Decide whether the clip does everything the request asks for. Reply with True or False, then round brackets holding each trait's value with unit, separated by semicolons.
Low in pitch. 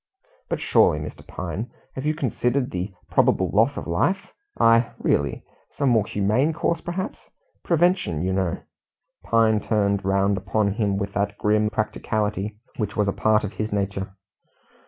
True (105 Hz)